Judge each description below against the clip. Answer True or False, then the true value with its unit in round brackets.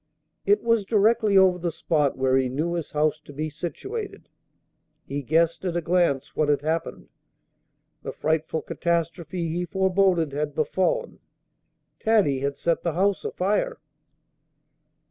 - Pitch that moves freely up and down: False (4.0 semitones)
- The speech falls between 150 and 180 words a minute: False (140 wpm)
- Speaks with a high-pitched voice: False (170 Hz)